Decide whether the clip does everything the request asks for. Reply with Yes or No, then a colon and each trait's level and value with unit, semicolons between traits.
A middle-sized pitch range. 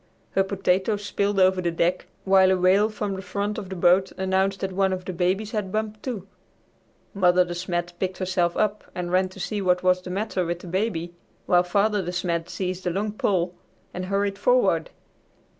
No: narrow, 1.9 semitones